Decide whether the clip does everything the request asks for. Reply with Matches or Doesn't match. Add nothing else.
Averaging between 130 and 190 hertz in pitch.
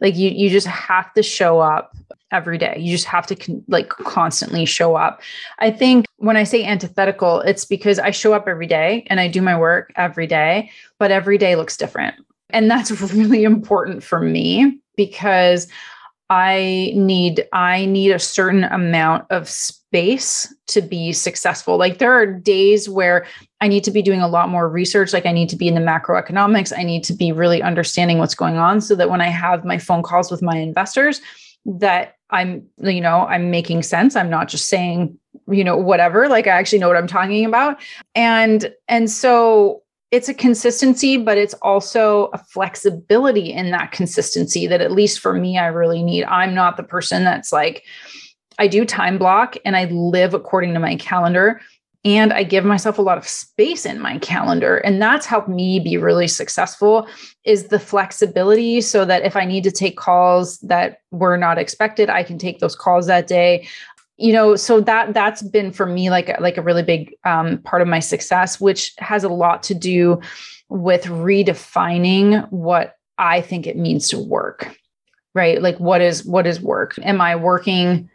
Matches